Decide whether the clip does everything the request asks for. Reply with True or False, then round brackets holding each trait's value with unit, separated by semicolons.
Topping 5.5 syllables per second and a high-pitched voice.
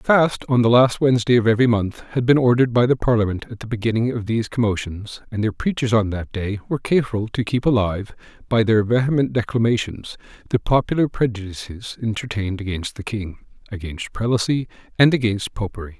False (6.0 syllables/s; 115 Hz)